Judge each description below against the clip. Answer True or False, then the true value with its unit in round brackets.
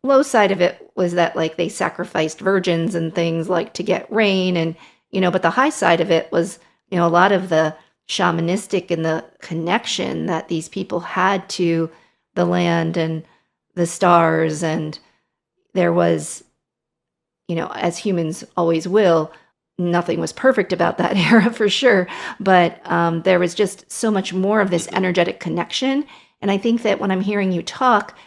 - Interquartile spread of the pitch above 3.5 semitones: False (2.8 semitones)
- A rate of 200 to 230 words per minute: False (180 wpm)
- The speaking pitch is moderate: True (175 Hz)